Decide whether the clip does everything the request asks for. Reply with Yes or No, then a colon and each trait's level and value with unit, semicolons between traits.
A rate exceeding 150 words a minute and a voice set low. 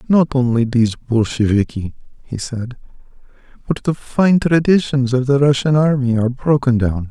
No: average, 145 wpm; low, 130 Hz